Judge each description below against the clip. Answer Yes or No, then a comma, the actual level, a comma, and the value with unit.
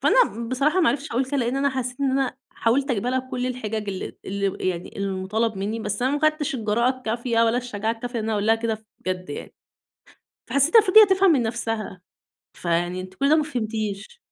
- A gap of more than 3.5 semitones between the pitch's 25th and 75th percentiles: Yes, average, 4.2 semitones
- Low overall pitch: No, high, 235 Hz